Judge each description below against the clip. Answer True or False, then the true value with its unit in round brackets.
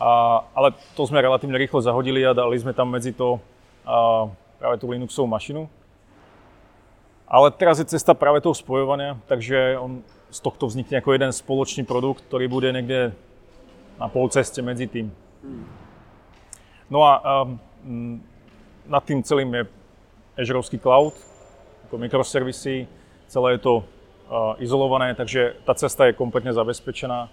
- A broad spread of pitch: False (2.7 semitones)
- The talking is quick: False (135 wpm)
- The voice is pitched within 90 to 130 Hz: True (125 Hz)